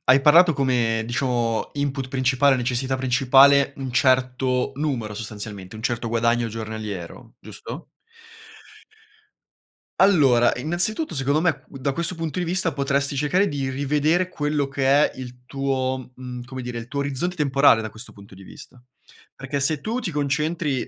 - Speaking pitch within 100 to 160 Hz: Yes, low, 135 Hz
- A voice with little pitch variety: No, average, 3.2 semitones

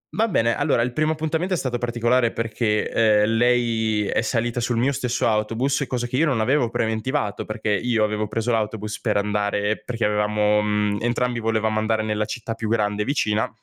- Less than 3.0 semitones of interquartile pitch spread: Yes, narrow, 2.4 semitones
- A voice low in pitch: Yes, low, 115 Hz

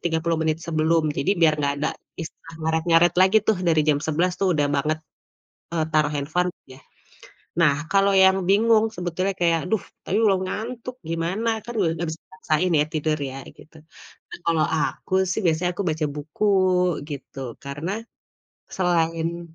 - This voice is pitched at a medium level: Yes, medium, 165 Hz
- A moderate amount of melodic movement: Yes, average, 3.3 semitones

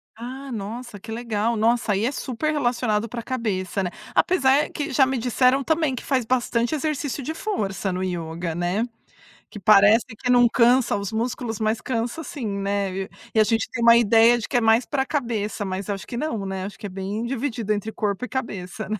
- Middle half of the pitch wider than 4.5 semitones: No, average, 3.8 semitones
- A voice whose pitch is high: Yes, high, 230 Hz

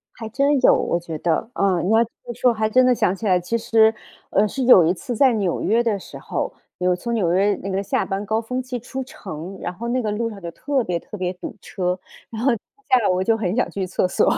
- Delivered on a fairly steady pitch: No, average, 4.4 semitones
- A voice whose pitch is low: No, high, 215 Hz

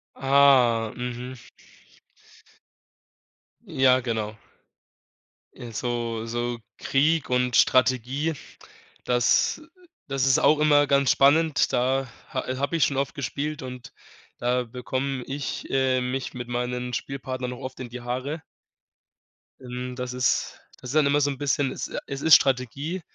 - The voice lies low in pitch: Yes, low, 130 Hz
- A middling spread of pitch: No, narrow, 2.1 semitones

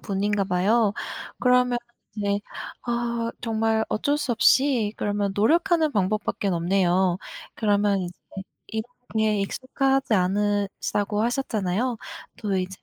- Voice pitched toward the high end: Yes, high, 210 Hz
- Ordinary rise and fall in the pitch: Yes, average, 3.3 semitones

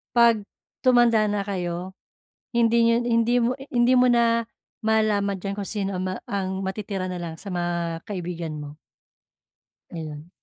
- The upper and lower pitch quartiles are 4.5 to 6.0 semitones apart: Yes, average, 4.8 semitones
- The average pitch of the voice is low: No, high, 200 Hz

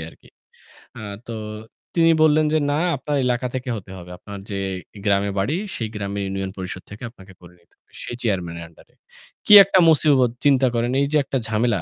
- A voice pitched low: Yes, low, 110 Hz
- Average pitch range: No, wide, 5.8 semitones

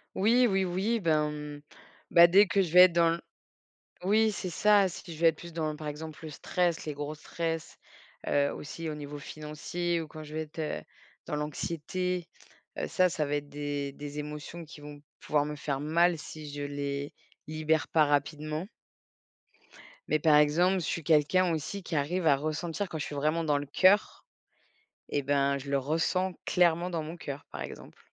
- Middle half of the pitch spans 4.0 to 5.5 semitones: No, average, 2.9 semitones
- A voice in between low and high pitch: Yes, medium, 155 Hz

